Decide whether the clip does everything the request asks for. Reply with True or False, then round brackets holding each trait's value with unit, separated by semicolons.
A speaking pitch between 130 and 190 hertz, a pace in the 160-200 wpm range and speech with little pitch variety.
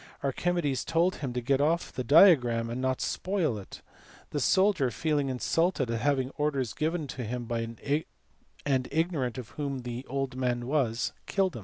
False (135 Hz; 165 wpm; 4.3 semitones)